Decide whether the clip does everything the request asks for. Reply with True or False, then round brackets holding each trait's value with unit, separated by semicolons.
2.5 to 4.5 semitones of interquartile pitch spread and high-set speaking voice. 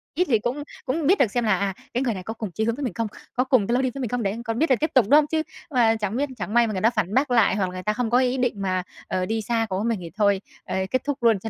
True (3.8 semitones; 230 Hz)